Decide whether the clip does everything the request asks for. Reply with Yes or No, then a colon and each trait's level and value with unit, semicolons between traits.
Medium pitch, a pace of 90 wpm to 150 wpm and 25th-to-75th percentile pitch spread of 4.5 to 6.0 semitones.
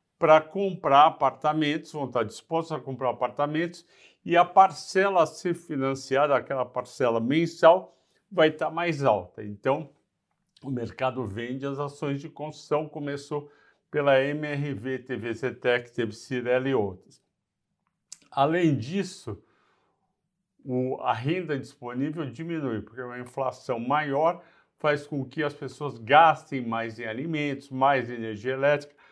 No: medium, 145 Hz; average, 125 wpm; average, 3.6 semitones